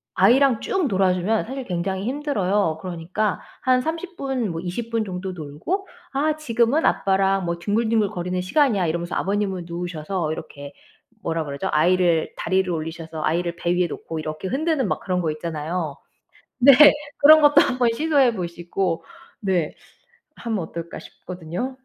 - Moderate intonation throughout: No, wide, 5.8 semitones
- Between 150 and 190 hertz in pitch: Yes, medium, 185 Hz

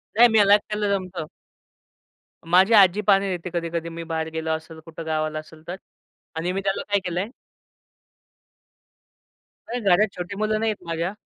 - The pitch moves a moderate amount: Yes, average, 3.5 semitones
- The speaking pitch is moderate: Yes, medium, 180 Hz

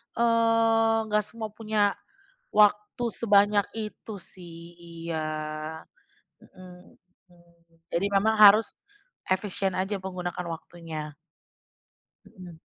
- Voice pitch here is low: No, high, 190 Hz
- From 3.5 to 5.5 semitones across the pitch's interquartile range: Yes, average, 4.0 semitones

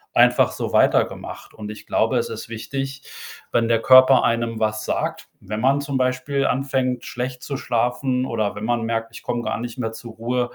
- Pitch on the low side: Yes, low, 120 Hz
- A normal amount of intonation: No, narrow, 2.3 semitones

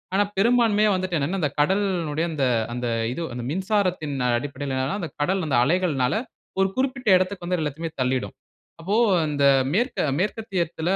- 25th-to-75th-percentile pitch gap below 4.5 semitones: No, average, 5.0 semitones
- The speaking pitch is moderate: Yes, medium, 175 Hz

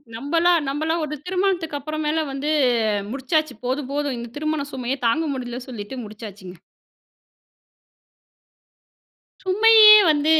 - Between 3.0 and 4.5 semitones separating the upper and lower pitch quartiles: Yes, average, 4.2 semitones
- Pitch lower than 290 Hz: No, very high, 295 Hz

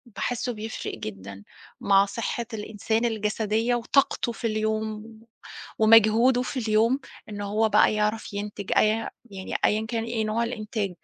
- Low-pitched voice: No, high, 220 Hz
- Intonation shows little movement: Yes, narrow, 1.7 semitones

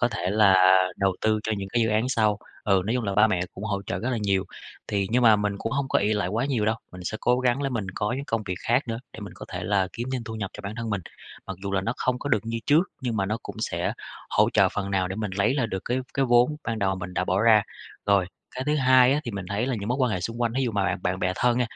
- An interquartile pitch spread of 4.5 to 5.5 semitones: No, average, 3.7 semitones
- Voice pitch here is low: Yes, low, 110 Hz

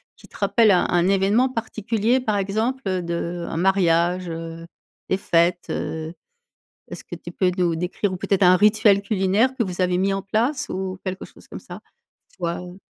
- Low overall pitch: No, high, 190 Hz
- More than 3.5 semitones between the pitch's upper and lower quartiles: No, average, 3.0 semitones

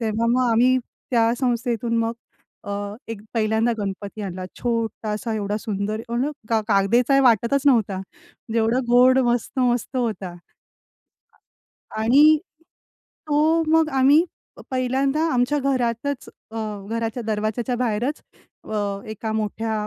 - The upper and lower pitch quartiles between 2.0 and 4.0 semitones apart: Yes, average, 2.9 semitones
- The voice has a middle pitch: No, high, 235 Hz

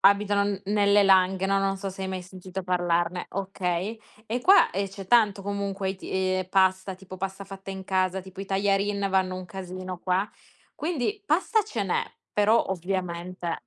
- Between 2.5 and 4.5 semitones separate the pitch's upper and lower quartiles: No, narrow, 1.3 semitones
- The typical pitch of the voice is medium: No, high, 195 Hz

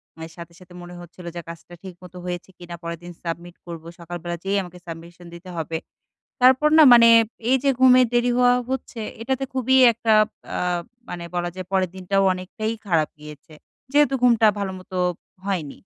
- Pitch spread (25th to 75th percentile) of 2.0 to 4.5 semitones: No, average, 5.2 semitones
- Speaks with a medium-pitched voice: Yes, medium, 180 Hz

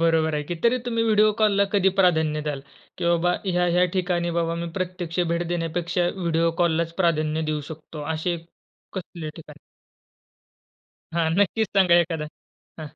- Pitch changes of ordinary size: No, narrow, 2.1 semitones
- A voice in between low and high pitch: Yes, medium, 170 Hz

